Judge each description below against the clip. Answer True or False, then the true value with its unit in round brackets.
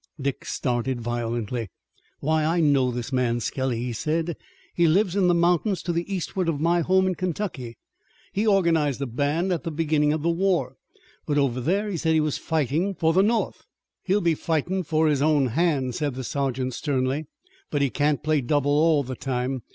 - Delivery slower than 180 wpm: False (195 wpm)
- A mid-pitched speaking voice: True (150 Hz)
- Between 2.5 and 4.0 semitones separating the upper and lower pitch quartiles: False (4.5 semitones)